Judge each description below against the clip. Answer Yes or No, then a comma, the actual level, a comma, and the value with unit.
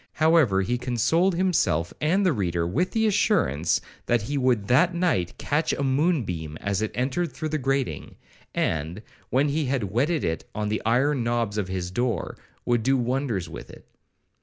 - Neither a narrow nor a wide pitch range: No, wide, 7.1 semitones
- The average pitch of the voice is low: Yes, low, 125 Hz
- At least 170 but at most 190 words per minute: Yes, average, 180 wpm